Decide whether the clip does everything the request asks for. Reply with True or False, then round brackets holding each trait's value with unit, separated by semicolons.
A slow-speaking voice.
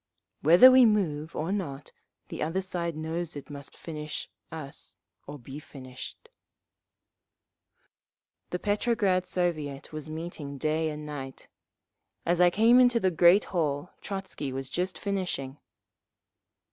True (125 wpm)